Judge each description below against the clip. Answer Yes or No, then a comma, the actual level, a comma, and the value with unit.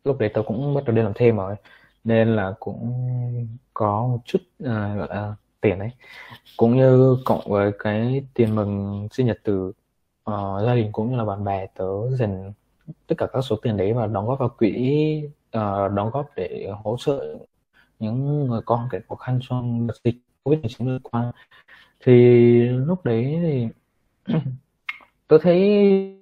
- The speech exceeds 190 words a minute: No, average, 175 wpm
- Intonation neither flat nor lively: Yes, average, 3.5 semitones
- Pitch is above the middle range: No, low, 120 Hz